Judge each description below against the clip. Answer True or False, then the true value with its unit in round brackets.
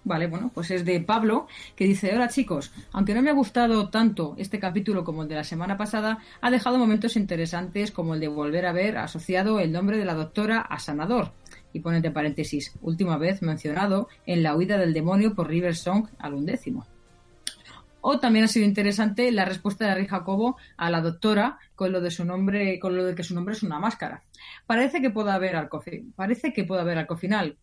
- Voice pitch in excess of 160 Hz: True (190 Hz)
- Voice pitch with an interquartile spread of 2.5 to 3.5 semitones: False (4.2 semitones)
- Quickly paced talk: True (200 wpm)